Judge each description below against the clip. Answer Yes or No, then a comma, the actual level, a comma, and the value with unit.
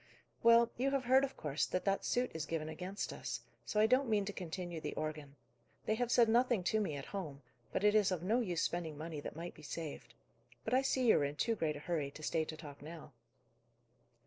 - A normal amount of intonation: No, wide, 6.6 semitones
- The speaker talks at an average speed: No, fast, 235 wpm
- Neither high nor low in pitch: Yes, medium, 180 Hz